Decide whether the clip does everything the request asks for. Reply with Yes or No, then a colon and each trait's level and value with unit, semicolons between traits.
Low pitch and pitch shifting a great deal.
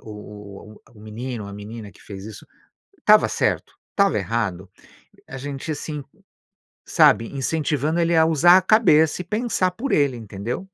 Yes: low, 130 Hz; wide, 7.3 semitones